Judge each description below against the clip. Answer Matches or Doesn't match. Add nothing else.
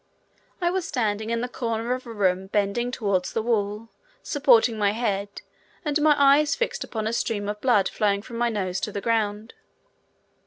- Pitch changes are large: Doesn't match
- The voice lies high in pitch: Matches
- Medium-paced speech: Matches